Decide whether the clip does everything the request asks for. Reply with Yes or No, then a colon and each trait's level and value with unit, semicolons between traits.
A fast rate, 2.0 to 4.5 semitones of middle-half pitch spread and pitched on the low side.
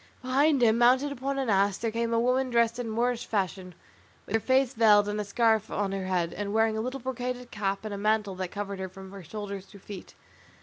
No: fast, 235 wpm; average, 3.6 semitones; high, 220 Hz